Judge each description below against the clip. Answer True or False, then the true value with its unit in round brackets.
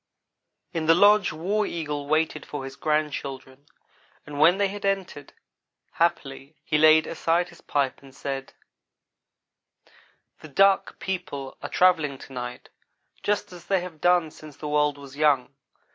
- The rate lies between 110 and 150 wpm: True (145 wpm)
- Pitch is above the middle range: False (155 Hz)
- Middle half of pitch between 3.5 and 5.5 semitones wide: True (3.9 semitones)